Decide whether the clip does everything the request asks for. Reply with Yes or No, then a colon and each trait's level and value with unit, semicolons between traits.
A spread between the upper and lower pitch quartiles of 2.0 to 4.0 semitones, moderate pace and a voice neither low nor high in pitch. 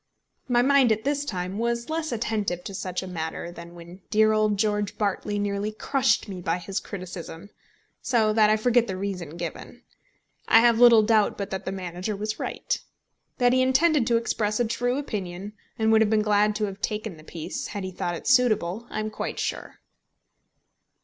No: average, 3.7 semitones; average, 195 wpm; high, 210 Hz